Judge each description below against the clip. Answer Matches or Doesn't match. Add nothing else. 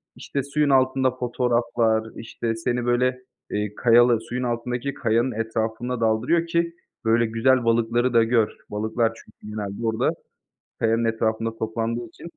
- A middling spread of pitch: Doesn't match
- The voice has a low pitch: Matches